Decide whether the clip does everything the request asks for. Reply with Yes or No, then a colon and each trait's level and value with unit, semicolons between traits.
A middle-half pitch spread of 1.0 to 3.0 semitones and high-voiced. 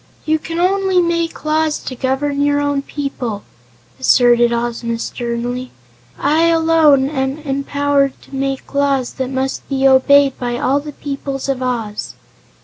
Yes: narrow, 2.4 semitones; very high, 275 Hz